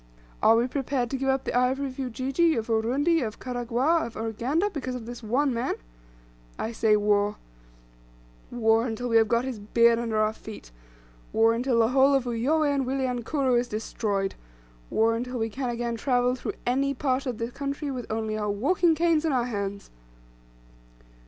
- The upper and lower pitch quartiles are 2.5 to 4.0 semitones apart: Yes, average, 3.2 semitones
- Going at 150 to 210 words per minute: Yes, average, 180 wpm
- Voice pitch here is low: No, high, 245 Hz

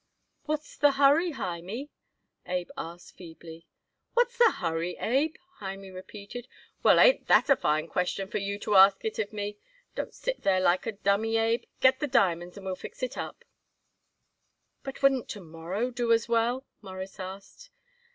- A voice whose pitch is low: No, high, 205 Hz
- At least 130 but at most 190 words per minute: Yes, average, 165 wpm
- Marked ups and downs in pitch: Yes, wide, 5.7 semitones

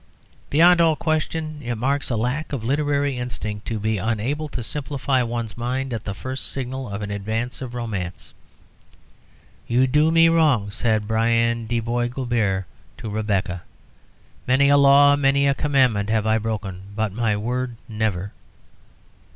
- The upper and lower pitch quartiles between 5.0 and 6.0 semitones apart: No, average, 4.3 semitones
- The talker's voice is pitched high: No, low, 120 Hz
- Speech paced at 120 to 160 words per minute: Yes, average, 155 wpm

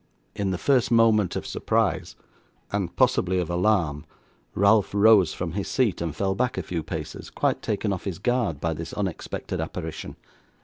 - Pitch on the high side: No, very low, 95 Hz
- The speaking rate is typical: Yes, average, 170 wpm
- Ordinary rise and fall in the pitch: Yes, average, 4.2 semitones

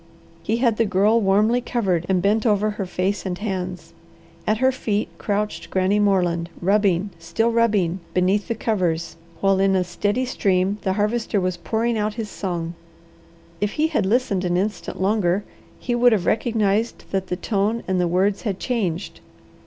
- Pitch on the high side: Yes, high, 200 Hz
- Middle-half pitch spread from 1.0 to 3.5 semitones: Yes, average, 3.1 semitones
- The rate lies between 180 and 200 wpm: No, average, 170 wpm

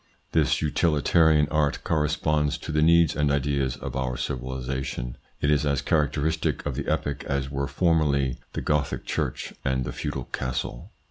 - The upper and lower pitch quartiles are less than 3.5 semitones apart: Yes, narrow, 2.4 semitones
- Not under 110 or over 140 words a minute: No, average, 155 wpm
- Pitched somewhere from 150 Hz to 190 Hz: No, very low, 70 Hz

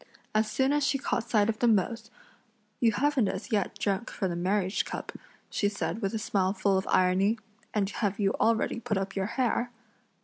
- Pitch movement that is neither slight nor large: Yes, average, 3.1 semitones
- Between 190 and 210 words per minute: Yes, average, 200 wpm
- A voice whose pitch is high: Yes, high, 210 Hz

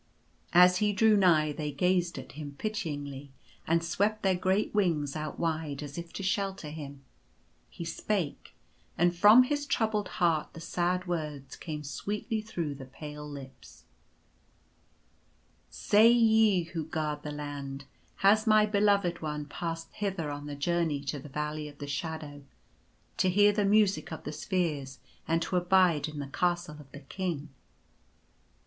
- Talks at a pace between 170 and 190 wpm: No, average, 155 wpm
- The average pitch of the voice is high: No, medium, 165 Hz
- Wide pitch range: No, average, 4.7 semitones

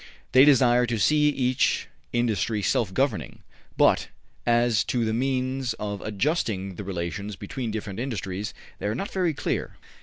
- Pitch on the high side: No, low, 115 Hz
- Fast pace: No, average, 150 wpm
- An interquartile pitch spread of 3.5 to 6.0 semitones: Yes, average, 4.2 semitones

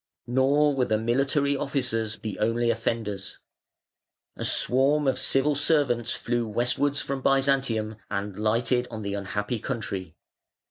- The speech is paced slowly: Yes, slow, 130 wpm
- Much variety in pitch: No, average, 3.9 semitones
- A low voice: Yes, low, 120 Hz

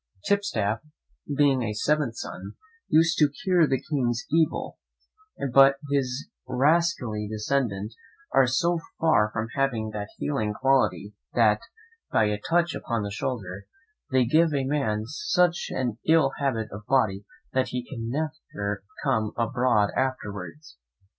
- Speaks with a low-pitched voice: Yes, low, 125 Hz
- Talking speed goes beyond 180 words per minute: No, slow, 135 wpm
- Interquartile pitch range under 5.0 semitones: No, wide, 5.5 semitones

